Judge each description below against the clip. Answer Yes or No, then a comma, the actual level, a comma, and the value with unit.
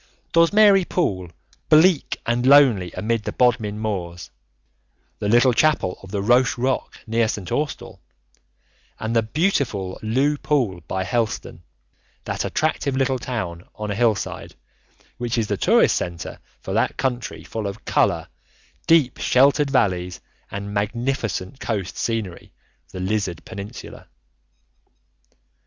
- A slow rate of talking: Yes, slow, 125 wpm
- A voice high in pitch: No, low, 115 Hz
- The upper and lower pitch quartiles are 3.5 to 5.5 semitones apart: Yes, average, 5.1 semitones